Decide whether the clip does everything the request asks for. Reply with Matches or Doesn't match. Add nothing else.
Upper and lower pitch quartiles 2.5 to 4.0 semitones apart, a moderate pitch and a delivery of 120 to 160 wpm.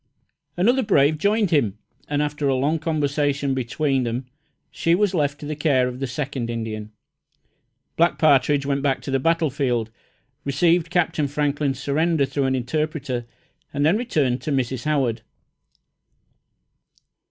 Matches